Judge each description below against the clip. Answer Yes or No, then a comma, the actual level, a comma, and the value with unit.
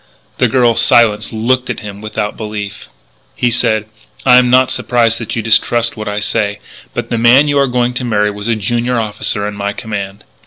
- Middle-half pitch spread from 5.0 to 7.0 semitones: No, average, 2.7 semitones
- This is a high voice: No, low, 115 Hz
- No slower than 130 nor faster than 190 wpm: No, average, 200 wpm